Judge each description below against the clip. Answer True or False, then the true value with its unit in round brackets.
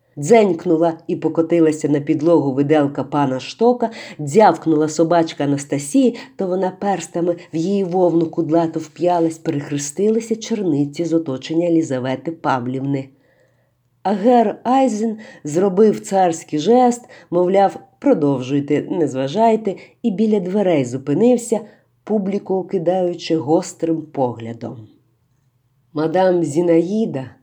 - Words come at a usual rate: False (95 wpm)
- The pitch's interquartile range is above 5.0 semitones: True (5.5 semitones)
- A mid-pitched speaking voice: True (165 Hz)